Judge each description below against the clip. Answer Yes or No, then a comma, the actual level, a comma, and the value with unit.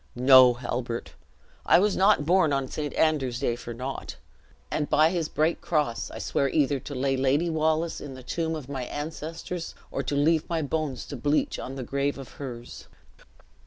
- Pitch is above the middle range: No, medium, 145 Hz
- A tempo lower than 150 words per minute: No, average, 180 wpm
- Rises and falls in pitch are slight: No, average, 3.4 semitones